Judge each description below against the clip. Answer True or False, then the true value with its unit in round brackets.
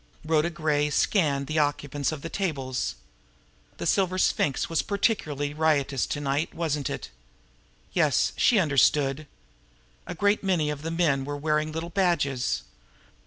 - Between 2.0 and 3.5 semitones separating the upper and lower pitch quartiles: True (2.9 semitones)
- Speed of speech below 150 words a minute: True (140 wpm)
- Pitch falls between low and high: True (150 Hz)